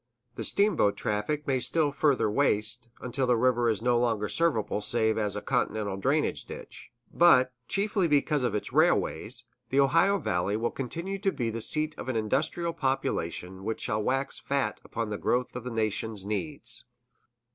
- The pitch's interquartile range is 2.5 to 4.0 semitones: No, average, 5.1 semitones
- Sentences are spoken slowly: No, average, 170 wpm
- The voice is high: No, low, 125 Hz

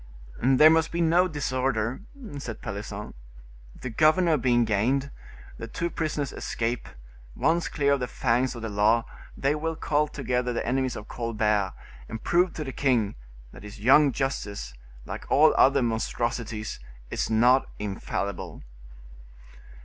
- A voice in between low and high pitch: No, low, 125 Hz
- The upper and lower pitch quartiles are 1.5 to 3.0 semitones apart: No, average, 4.6 semitones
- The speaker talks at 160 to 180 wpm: No, average, 140 wpm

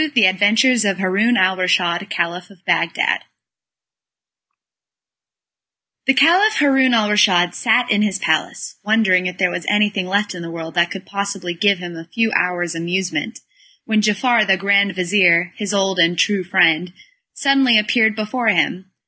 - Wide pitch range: No, average, 3.3 semitones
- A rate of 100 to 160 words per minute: Yes, average, 155 wpm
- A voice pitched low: No, high, 195 Hz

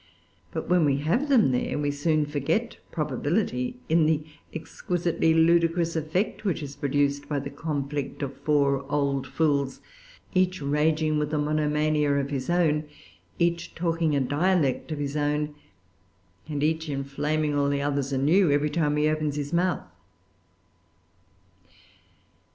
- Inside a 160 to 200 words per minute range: No, average, 140 wpm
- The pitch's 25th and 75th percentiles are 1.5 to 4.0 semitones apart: Yes, narrow, 2.4 semitones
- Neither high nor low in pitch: Yes, medium, 150 Hz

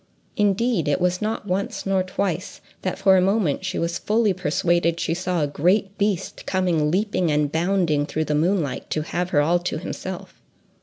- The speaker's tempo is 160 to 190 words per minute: Yes, average, 185 wpm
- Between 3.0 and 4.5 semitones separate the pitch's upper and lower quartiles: Yes, average, 3.4 semitones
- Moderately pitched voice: Yes, medium, 180 Hz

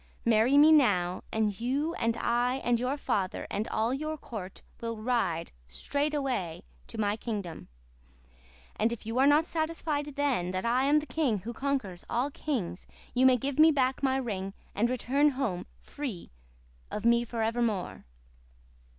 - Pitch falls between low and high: No, high, 240 Hz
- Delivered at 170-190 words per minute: No, average, 160 wpm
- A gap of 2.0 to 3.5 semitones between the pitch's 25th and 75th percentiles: No, average, 4.7 semitones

